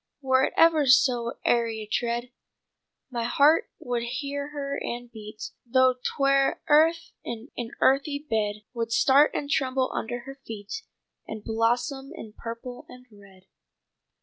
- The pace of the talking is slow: No, average, 145 wpm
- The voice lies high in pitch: Yes, very high, 250 Hz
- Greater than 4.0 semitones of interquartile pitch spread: No, average, 3.2 semitones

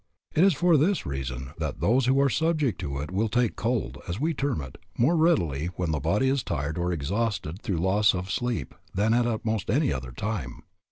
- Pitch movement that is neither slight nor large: No, wide, 8.1 semitones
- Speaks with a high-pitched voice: No, low, 110 Hz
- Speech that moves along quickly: Yes, fast, 215 wpm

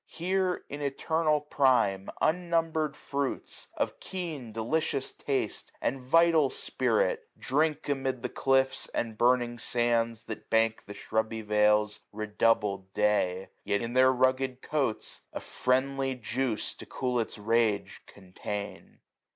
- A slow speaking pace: Yes, slow, 125 wpm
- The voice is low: Yes, low, 125 Hz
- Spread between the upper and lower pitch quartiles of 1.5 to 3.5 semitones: No, average, 4.6 semitones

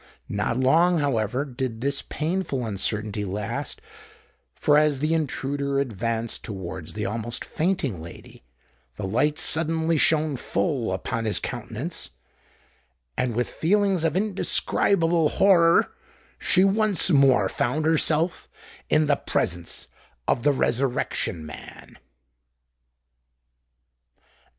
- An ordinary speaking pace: No, slow, 105 wpm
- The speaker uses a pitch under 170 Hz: Yes, medium, 140 Hz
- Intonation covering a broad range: Yes, wide, 6.8 semitones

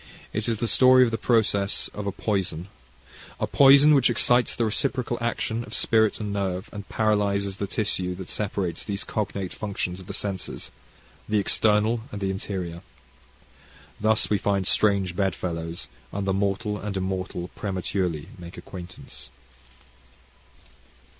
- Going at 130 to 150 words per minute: Yes, average, 145 wpm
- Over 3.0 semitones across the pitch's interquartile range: No, average, 2.7 semitones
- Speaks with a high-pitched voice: No, low, 100 Hz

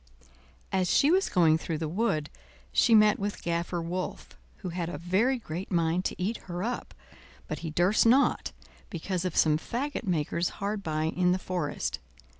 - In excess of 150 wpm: Yes, average, 175 wpm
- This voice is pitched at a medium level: Yes, medium, 180 Hz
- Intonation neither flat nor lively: Yes, average, 3.7 semitones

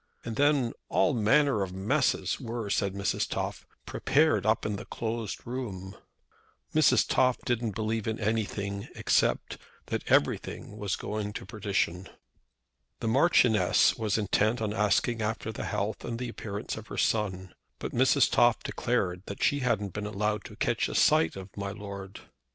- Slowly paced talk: No, average, 155 wpm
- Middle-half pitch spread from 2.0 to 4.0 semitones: Yes, average, 2.8 semitones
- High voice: No, low, 110 Hz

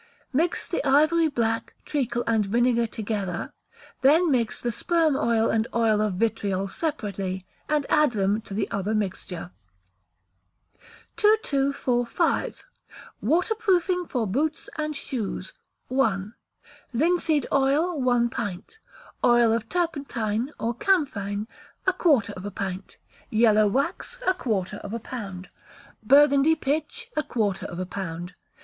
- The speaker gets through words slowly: Yes, slow, 125 wpm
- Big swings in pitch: Yes, wide, 6.7 semitones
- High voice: Yes, high, 235 Hz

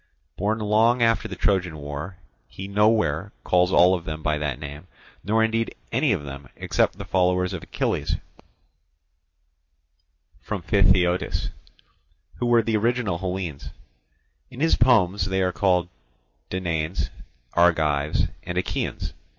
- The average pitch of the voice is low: Yes, very low, 90 Hz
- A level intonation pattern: No, average, 4.6 semitones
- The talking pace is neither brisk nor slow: No, slow, 130 wpm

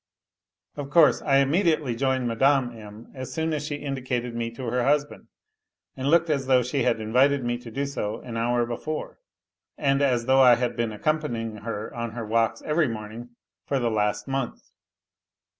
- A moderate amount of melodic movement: Yes, average, 3.3 semitones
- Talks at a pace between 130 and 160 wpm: No, average, 180 wpm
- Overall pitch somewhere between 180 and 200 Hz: No, low, 125 Hz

